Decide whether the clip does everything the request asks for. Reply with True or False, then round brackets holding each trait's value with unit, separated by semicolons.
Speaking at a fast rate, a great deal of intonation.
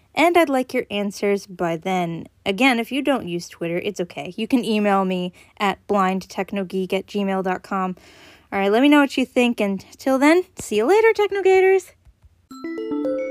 False (170 wpm; 5.9 semitones)